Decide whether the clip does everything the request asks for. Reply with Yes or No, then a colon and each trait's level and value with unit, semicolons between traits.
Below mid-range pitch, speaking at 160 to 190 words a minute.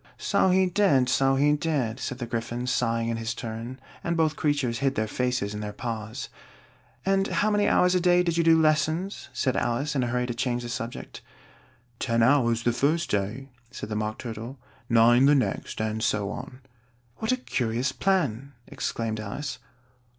Yes: low, 125 Hz; average, 185 wpm